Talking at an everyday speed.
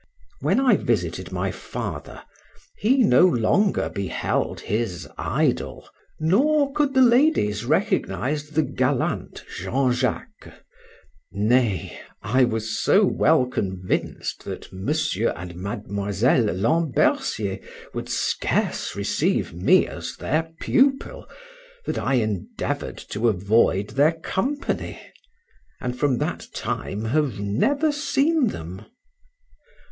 No: slow, 105 wpm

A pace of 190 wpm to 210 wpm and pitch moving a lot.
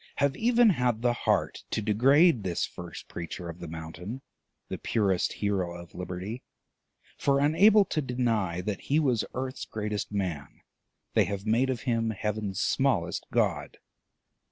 No: average, 150 wpm; wide, 6.0 semitones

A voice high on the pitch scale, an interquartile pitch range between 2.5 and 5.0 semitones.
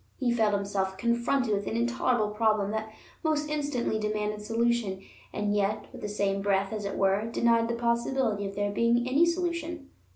Yes: high, 220 Hz; average, 2.8 semitones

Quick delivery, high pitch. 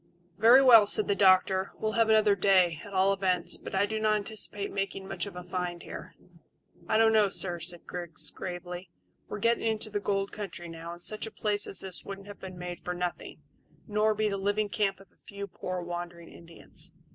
Yes: fast, 210 wpm; high, 195 Hz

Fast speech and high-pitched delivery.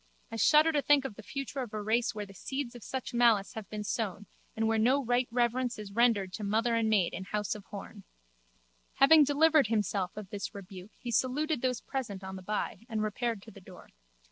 Yes: fast, 220 wpm; high, 225 Hz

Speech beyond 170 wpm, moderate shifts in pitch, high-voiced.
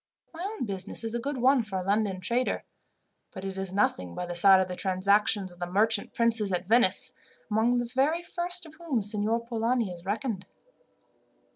Yes: average, 190 wpm; average, 4.3 semitones; high, 215 Hz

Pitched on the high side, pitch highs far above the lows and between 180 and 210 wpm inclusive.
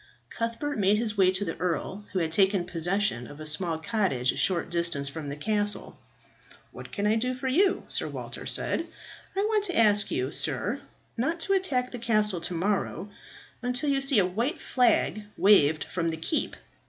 Yes: high, 205 Hz; wide, 6.6 semitones; average, 190 wpm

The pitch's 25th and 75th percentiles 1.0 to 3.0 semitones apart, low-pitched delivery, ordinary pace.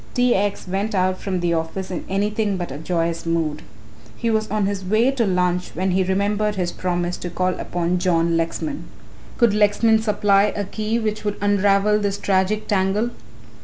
No: average, 2.7 semitones; high, 195 Hz; average, 180 wpm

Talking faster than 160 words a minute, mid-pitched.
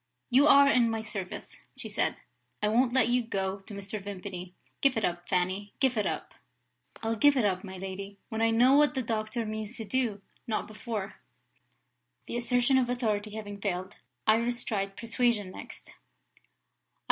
No: average, 170 wpm; high, 220 Hz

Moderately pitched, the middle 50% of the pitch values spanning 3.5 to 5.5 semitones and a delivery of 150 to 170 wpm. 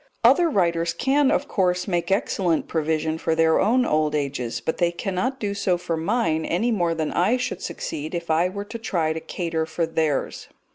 No: medium, 170 Hz; average, 3.9 semitones; average, 195 wpm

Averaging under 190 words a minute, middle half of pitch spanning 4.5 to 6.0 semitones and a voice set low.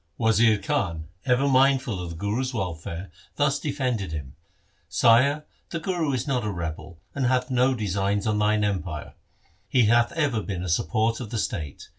Yes: average, 175 wpm; wide, 5.6 semitones; low, 110 Hz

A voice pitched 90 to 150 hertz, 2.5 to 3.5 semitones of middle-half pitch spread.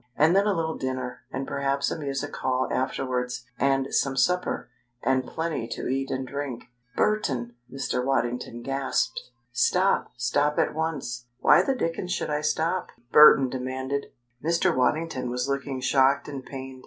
Yes: low, 135 Hz; average, 2.8 semitones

